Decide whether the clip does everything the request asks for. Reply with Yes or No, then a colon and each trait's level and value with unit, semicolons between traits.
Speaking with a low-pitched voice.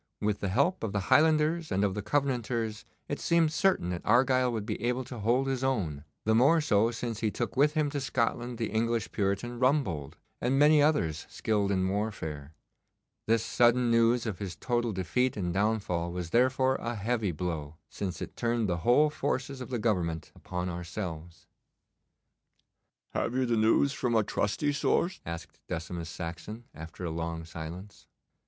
Yes: low, 110 Hz